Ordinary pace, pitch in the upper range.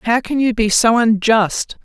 Yes: average, 195 wpm; high, 225 Hz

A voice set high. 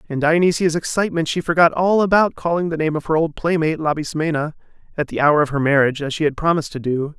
No: medium, 160 Hz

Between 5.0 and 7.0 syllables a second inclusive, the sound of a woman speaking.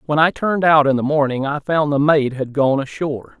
No: 5.6 syllables/s; male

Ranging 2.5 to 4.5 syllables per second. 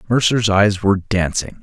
No: 4.9 syllables/s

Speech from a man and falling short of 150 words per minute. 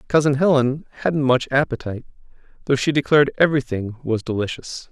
Yes: male; slow, 135 wpm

